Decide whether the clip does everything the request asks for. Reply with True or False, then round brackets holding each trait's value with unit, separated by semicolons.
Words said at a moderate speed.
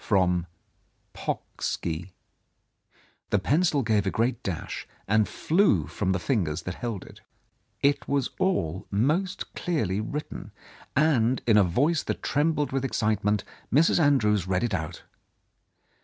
False (130 wpm)